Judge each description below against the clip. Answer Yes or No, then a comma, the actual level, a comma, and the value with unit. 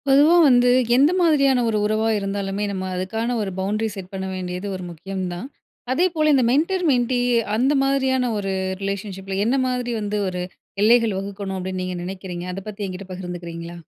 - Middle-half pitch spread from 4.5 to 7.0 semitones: Yes, average, 4.9 semitones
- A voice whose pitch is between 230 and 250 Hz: No, high, 205 Hz